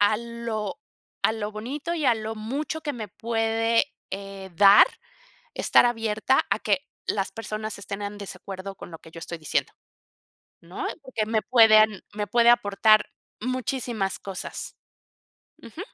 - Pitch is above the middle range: Yes, high, 215 Hz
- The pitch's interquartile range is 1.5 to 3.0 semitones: Yes, narrow, 2.5 semitones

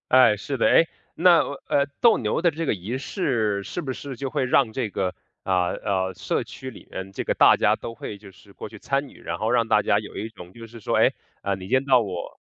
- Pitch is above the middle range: No, low, 115 Hz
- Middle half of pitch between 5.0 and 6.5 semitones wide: Yes, wide, 5.4 semitones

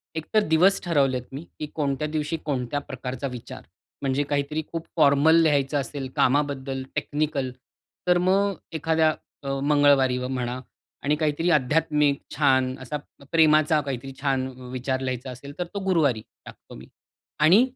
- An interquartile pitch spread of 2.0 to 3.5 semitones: Yes, average, 3.0 semitones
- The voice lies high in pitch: No, medium, 145 Hz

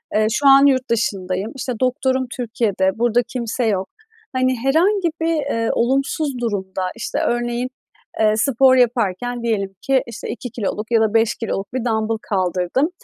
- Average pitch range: Yes, average, 3.3 semitones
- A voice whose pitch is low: No, high, 235 Hz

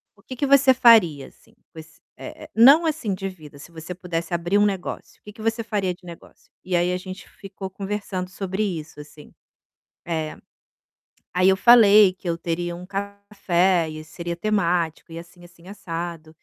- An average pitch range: Yes, average, 3.2 semitones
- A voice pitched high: No, medium, 180 Hz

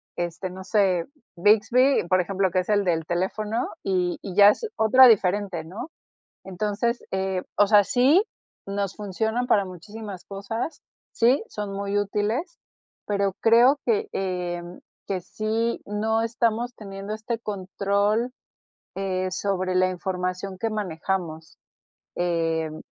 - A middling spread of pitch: Yes, average, 3.2 semitones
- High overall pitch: Yes, high, 200 Hz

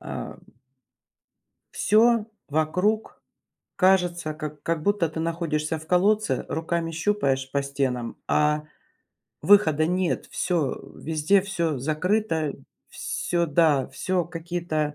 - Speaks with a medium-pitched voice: Yes, medium, 165 Hz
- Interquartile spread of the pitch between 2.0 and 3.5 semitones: Yes, average, 3.1 semitones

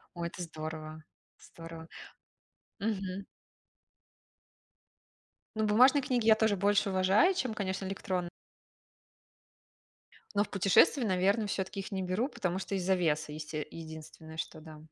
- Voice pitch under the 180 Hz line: No, high, 190 Hz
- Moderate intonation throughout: Yes, average, 4.1 semitones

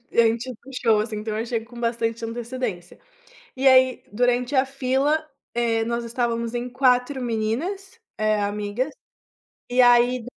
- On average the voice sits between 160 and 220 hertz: No, high, 240 Hz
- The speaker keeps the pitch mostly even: Yes, narrow, 2.3 semitones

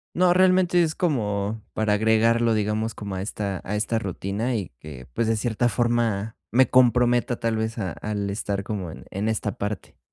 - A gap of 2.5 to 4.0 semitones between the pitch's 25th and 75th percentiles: Yes, average, 2.8 semitones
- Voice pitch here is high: No, low, 110 Hz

